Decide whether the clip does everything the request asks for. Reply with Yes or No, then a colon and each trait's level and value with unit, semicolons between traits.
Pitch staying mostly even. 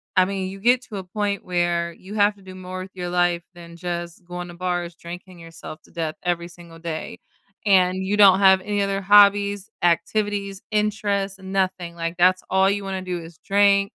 Yes: narrow, 2.3 semitones